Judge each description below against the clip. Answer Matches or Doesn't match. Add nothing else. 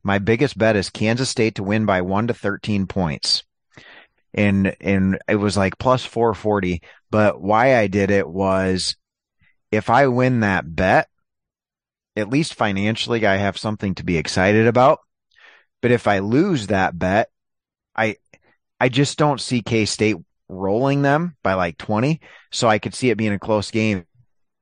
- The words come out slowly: Doesn't match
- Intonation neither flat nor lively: Matches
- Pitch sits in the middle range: Doesn't match